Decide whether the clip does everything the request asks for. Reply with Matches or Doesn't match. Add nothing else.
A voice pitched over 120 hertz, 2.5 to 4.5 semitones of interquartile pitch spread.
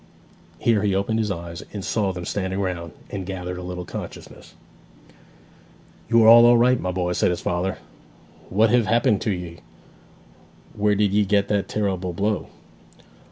Doesn't match